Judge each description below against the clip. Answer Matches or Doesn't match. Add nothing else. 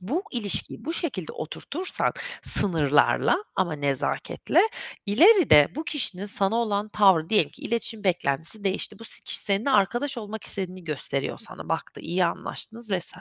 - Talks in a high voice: Matches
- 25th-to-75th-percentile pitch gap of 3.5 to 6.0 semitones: Matches